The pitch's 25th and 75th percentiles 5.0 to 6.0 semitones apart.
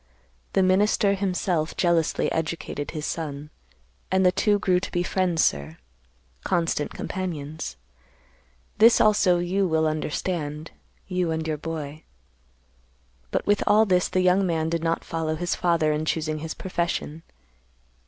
No: average, 2.9 semitones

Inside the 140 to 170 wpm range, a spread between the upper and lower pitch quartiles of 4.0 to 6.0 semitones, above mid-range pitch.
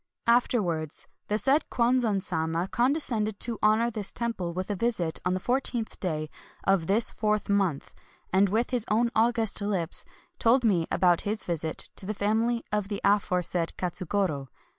Yes: average, 165 wpm; average, 4.4 semitones; high, 205 Hz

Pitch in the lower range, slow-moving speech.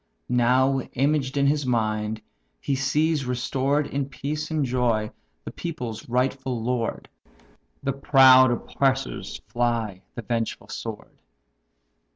Yes: low, 130 Hz; slow, 115 wpm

